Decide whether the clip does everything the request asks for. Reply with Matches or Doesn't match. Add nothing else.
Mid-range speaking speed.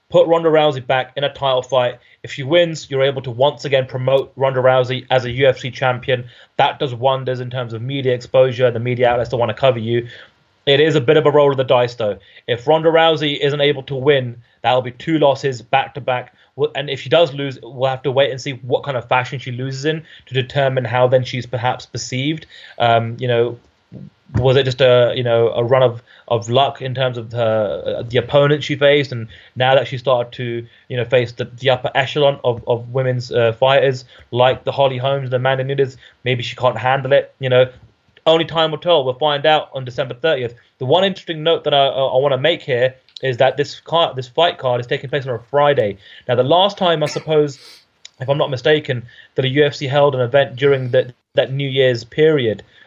Doesn't match